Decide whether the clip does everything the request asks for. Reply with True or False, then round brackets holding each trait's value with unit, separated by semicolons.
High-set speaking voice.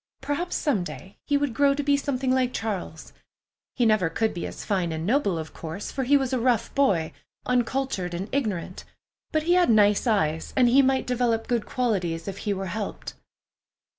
True (230 Hz)